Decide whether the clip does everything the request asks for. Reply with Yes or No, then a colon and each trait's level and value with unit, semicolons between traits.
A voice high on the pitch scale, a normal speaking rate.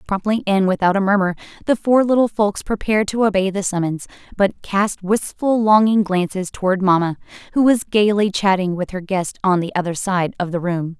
Yes: high, 195 Hz; average, 190 wpm